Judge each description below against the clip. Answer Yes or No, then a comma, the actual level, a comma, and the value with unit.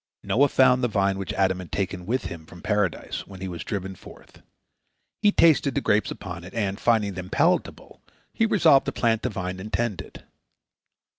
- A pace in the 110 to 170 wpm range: No, average, 195 wpm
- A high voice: No, low, 100 Hz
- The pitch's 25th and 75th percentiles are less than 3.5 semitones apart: No, average, 4.3 semitones